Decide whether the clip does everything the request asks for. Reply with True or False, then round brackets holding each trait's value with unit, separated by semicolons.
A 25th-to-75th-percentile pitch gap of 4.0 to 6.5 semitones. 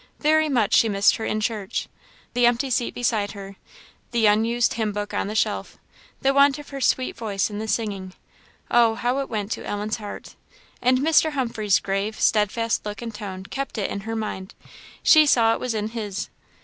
False (3.0 semitones)